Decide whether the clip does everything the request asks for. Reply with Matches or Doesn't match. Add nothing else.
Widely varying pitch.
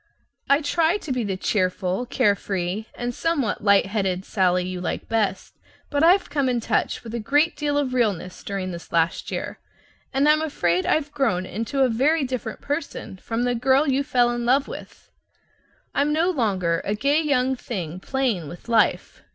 Matches